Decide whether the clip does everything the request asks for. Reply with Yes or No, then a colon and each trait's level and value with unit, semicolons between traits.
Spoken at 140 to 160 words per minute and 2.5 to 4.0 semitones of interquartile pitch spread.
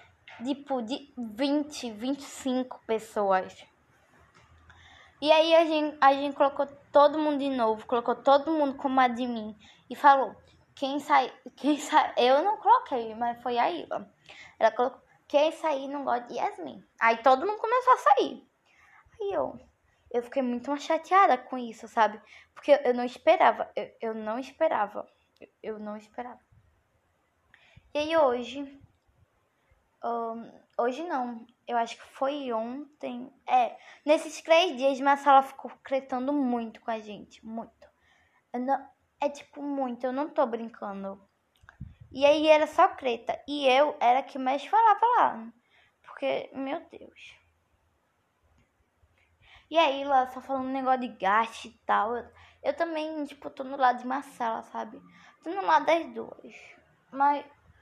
Yes: average, 150 wpm; average, 3.4 semitones